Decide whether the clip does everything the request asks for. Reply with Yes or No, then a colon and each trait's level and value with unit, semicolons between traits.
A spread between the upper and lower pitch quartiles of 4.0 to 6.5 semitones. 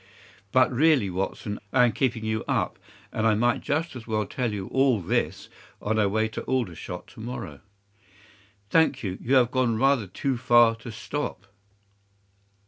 No: average, 3.4 semitones